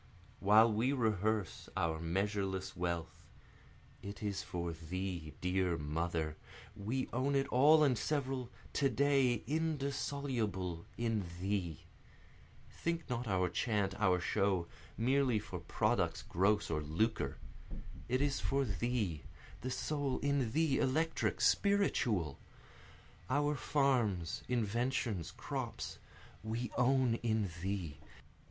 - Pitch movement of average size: No, wide, 6.5 semitones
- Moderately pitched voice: No, low, 110 Hz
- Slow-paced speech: Yes, slow, 110 wpm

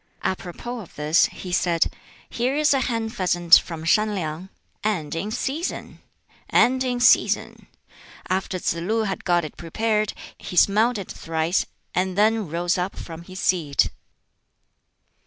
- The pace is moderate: Yes, average, 145 wpm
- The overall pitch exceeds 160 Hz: Yes, high, 190 Hz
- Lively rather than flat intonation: No, average, 4.6 semitones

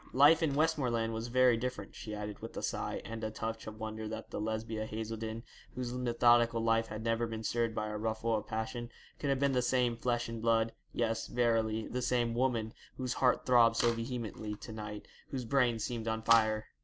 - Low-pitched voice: Yes, low, 115 Hz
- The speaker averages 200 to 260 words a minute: Yes, fast, 205 wpm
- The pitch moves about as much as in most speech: No, narrow, 1.7 semitones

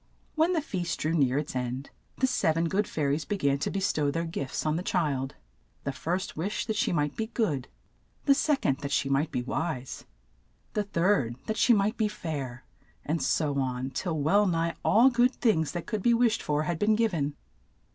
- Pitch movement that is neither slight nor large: No, wide, 6.8 semitones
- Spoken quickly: Yes, fast, 215 wpm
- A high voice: No, medium, 165 Hz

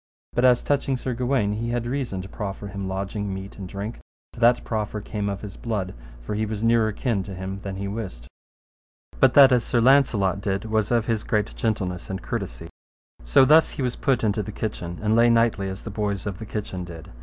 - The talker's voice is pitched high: No, low, 105 Hz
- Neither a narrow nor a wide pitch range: Yes, average, 3.2 semitones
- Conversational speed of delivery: No, fast, 220 wpm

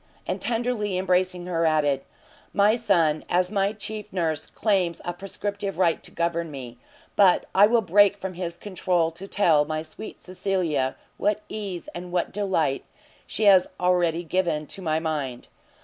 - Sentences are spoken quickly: No, average, 160 wpm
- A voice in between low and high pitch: Yes, medium, 180 Hz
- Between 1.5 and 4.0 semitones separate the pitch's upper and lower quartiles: Yes, average, 3.6 semitones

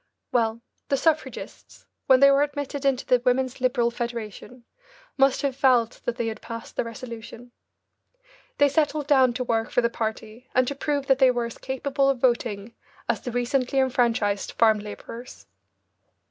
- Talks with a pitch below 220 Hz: No, very high, 250 Hz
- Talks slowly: No, average, 165 wpm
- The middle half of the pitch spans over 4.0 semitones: No, narrow, 2.5 semitones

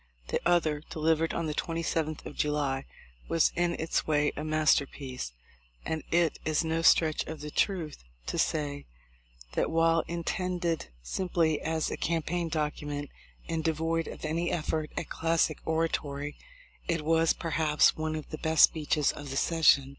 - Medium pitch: Yes, medium, 160 Hz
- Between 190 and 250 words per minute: No, average, 165 wpm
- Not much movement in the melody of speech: Yes, narrow, 1.7 semitones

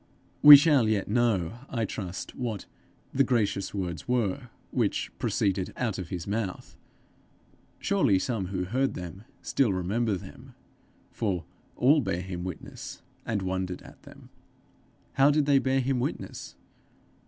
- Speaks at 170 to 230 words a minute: No, average, 140 wpm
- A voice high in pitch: No, low, 105 Hz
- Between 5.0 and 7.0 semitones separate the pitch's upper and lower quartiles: Yes, average, 5.3 semitones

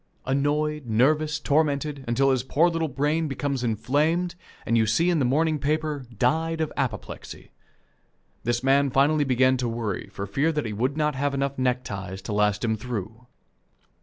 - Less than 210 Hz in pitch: Yes, low, 135 Hz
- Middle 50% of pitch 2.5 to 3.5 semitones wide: No, average, 4.2 semitones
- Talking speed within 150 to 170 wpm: Yes, average, 165 wpm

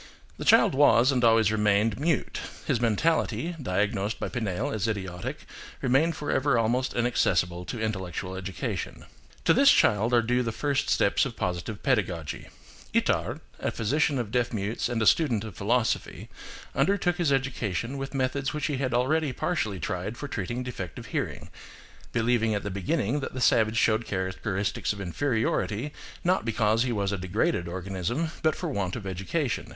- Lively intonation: No, average, 4.9 semitones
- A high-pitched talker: No, low, 115 Hz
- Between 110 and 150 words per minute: No, average, 165 wpm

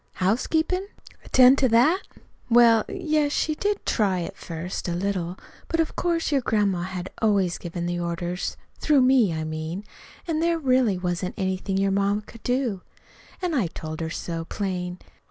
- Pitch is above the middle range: Yes, high, 200 Hz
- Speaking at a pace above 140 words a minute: Yes, average, 175 wpm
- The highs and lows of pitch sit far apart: Yes, wide, 6.9 semitones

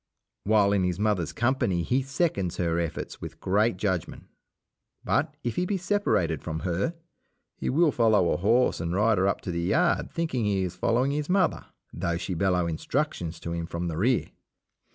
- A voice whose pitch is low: Yes, low, 100 Hz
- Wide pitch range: Yes, wide, 6.6 semitones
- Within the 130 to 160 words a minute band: No, average, 180 wpm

